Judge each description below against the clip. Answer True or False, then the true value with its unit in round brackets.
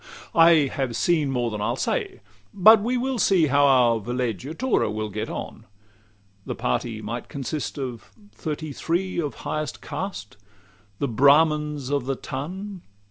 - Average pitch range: False (5.9 semitones)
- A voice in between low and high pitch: True (145 Hz)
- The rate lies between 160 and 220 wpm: False (150 wpm)